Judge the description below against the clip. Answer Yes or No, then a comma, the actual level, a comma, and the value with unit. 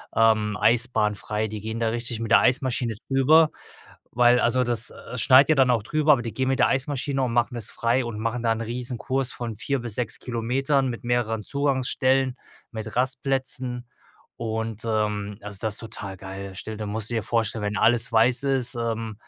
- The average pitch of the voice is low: Yes, low, 120 Hz